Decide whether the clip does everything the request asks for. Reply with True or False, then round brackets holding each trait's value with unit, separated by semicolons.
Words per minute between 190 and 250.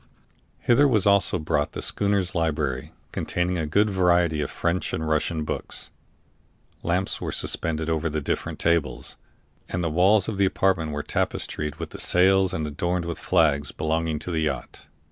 False (170 wpm)